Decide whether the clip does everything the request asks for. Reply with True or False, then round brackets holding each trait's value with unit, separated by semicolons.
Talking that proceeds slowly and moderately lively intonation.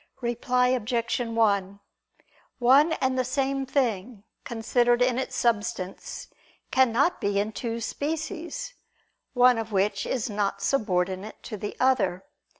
True (125 wpm; 4.0 semitones)